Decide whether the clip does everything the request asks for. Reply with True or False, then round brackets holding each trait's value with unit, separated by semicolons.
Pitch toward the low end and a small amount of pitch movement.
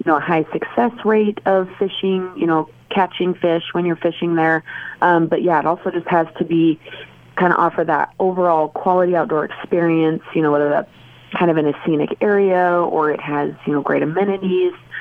False (170 Hz; 2.3 semitones)